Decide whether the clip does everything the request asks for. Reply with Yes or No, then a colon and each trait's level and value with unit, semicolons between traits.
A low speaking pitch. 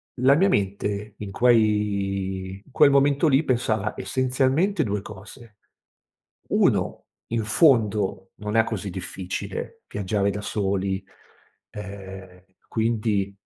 Yes: low, 105 Hz